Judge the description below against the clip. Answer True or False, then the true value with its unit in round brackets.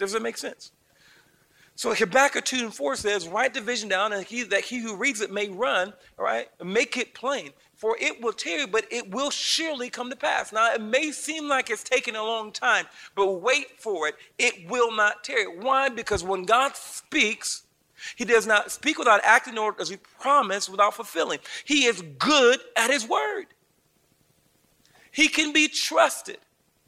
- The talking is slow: False (190 wpm)